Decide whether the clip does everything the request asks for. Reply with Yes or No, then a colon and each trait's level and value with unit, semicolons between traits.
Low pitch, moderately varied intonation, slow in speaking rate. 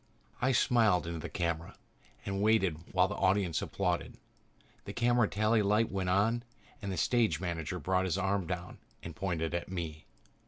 No: very low, 95 Hz; average, 3.5 semitones; average, 165 wpm